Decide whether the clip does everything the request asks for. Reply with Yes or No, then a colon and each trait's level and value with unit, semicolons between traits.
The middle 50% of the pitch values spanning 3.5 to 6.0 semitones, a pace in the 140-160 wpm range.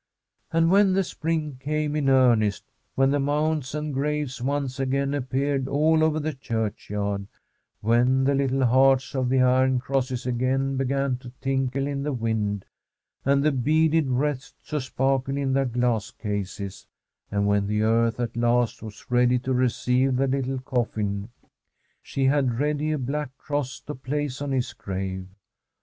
No: average, 2.7 semitones; average, 155 wpm